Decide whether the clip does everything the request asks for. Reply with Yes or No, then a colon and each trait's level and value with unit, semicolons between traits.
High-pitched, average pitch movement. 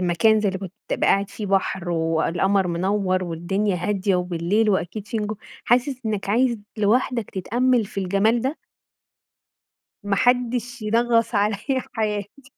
Yes: high, 205 Hz; average, 3.4 semitones